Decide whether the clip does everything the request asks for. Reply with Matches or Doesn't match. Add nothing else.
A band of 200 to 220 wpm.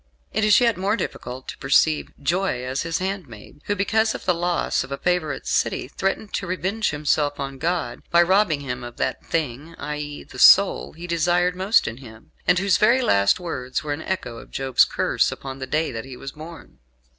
Matches